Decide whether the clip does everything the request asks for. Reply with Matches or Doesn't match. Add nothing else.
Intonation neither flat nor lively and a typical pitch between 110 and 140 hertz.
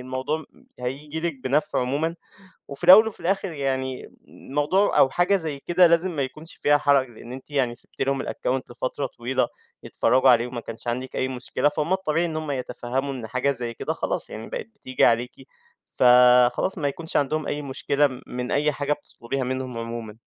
Matches